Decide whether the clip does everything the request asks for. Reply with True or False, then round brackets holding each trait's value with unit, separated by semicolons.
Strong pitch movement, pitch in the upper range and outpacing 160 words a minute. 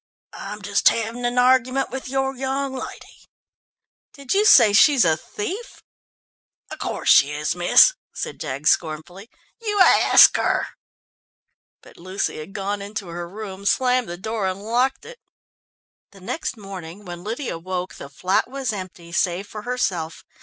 False (6.2 semitones; 205 Hz; 155 wpm)